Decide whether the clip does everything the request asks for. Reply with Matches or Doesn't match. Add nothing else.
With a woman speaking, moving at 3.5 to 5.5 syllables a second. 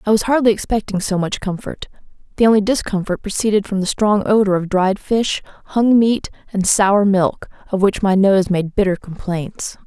Matches